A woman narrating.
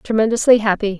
Yes: female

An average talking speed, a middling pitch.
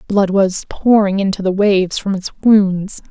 No: average, 175 wpm; high, 195 Hz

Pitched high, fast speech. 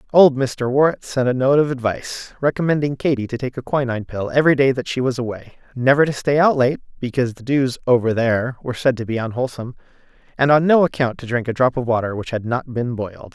No: low, 125 Hz; fast, 230 wpm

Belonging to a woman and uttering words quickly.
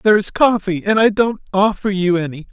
No: male; fast, 215 wpm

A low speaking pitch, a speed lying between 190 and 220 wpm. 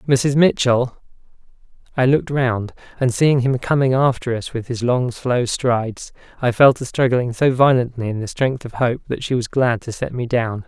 Yes: low, 125 Hz; average, 195 wpm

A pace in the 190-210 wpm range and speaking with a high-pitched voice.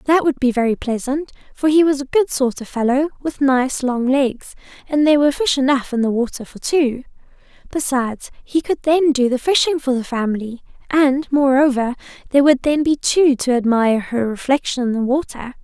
Yes: average, 195 wpm; very high, 270 Hz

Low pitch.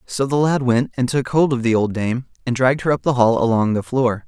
Yes: low, 125 Hz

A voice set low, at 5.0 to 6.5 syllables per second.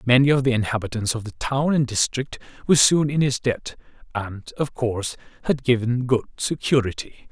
Yes: low, 125 Hz; 5.5 syllables/s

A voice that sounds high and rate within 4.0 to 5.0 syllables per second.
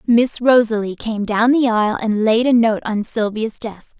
Yes: high, 225 Hz; 4.6 syllables/s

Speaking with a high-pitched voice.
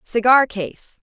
Yes: high, 235 Hz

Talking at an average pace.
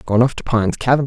No: fast, 280 wpm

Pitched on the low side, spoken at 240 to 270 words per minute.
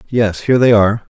No: low, 110 Hz; fast, 210 wpm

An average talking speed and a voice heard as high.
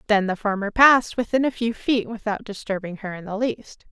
No: fast, 215 wpm; high, 215 Hz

